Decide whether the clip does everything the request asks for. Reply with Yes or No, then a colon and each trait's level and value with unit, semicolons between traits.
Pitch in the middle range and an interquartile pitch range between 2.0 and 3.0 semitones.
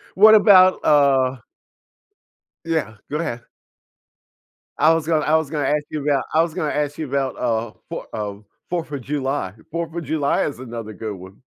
No: medium, 145 Hz; average, 4.0 semitones